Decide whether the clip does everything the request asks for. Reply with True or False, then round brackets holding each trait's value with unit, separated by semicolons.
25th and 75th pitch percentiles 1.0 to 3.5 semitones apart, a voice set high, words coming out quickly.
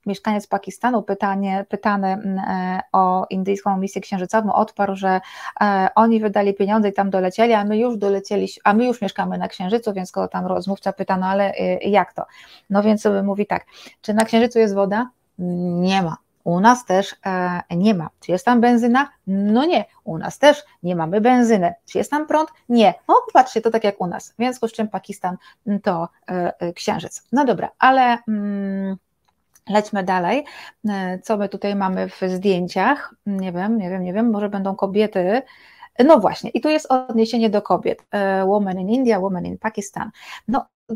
True (3.0 semitones; 200 Hz; 180 wpm)